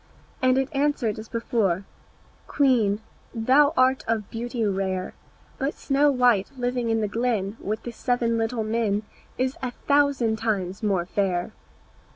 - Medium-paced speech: Yes, average, 145 wpm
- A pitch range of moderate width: Yes, average, 3.6 semitones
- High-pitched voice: Yes, high, 230 Hz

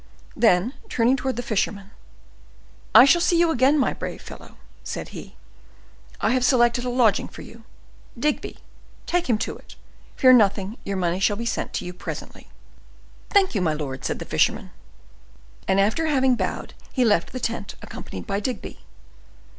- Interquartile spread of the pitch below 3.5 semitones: No, average, 4.6 semitones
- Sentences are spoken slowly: No, average, 165 wpm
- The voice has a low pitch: No, high, 235 Hz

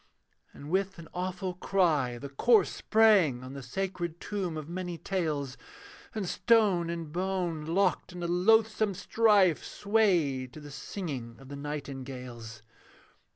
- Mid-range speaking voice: Yes, medium, 170 Hz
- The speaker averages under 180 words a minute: Yes, average, 140 wpm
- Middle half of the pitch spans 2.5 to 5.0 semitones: No, wide, 5.4 semitones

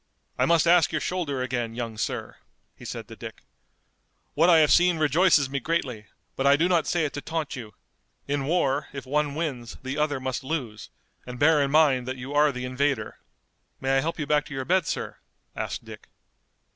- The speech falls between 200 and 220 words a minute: Yes, fast, 205 wpm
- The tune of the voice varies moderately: Yes, average, 3.5 semitones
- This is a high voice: No, medium, 145 Hz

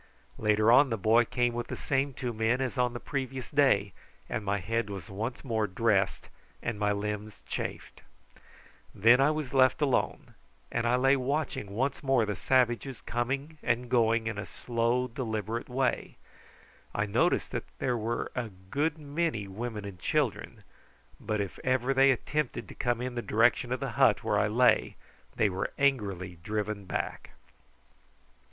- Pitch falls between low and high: No, low, 120 Hz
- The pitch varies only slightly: No, average, 3.6 semitones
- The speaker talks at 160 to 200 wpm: Yes, average, 165 wpm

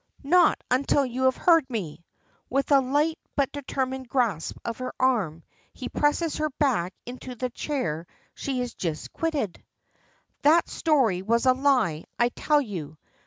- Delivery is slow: No, average, 155 wpm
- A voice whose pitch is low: No, very high, 255 Hz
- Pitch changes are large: No, average, 4.7 semitones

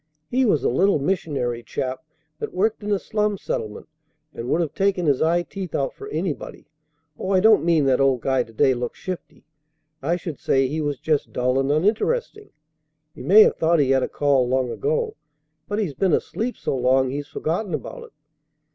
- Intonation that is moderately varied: No, wide, 6.6 semitones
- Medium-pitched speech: Yes, medium, 155 Hz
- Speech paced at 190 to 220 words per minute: Yes, average, 200 wpm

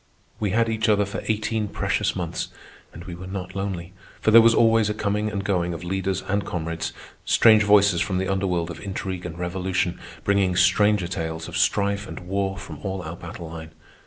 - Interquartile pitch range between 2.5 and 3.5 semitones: Yes, average, 2.8 semitones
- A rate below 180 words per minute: No, average, 195 wpm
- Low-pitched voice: Yes, very low, 95 Hz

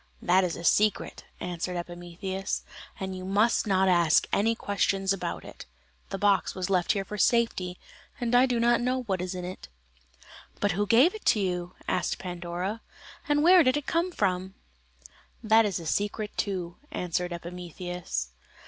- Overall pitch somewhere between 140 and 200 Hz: Yes, high, 190 Hz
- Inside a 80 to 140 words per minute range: No, average, 165 wpm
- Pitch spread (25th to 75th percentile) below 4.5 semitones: Yes, average, 3.6 semitones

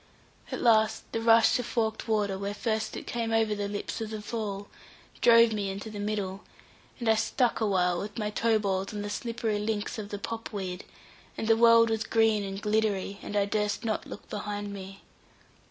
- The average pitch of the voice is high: Yes, high, 215 Hz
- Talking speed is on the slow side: No, average, 200 wpm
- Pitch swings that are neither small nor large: No, narrow, 1.8 semitones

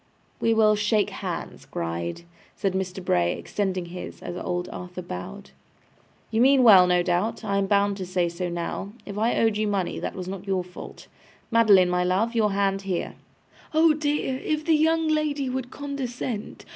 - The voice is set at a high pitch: Yes, high, 200 Hz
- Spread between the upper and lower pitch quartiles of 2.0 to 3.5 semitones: No, average, 4.8 semitones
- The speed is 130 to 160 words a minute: No, average, 180 wpm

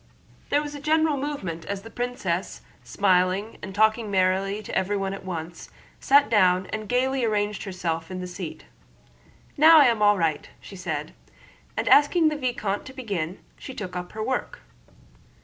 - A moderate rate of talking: Yes, average, 165 wpm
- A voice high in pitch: Yes, high, 205 Hz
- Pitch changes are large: Yes, wide, 5.7 semitones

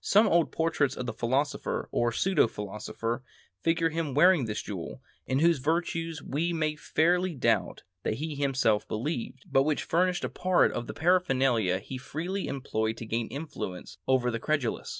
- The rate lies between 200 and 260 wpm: No, average, 165 wpm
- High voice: No, medium, 140 Hz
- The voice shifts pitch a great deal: Yes, wide, 5.8 semitones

